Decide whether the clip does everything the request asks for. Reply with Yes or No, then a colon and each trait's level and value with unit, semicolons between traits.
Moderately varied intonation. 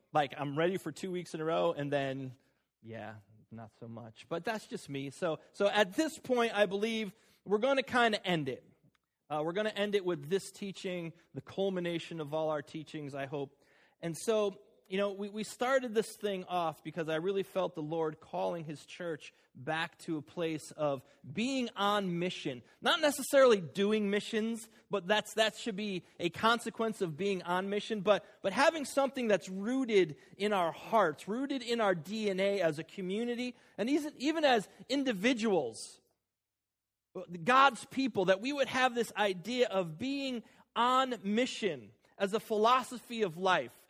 No: wide, 5.9 semitones